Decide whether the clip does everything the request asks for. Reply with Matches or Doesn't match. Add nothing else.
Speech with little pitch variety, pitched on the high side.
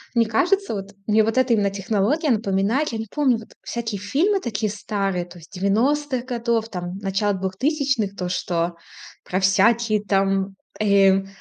Doesn't match